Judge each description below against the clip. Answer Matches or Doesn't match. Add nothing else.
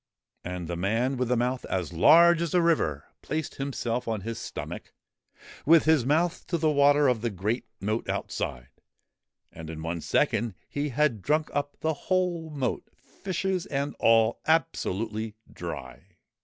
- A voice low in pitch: Matches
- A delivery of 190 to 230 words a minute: Doesn't match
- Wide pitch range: Matches